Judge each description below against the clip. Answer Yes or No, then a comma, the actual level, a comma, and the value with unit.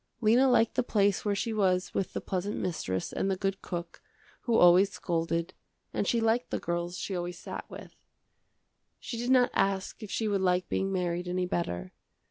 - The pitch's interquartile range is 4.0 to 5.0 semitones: No, average, 3.4 semitones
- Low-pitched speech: No, high, 190 Hz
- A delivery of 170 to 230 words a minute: Yes, average, 190 wpm